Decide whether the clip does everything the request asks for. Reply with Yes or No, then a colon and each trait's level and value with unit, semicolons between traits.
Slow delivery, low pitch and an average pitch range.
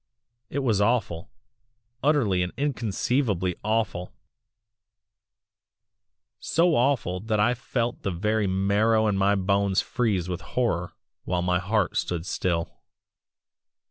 Yes: slow, 110 wpm; low, 100 Hz; average, 4.3 semitones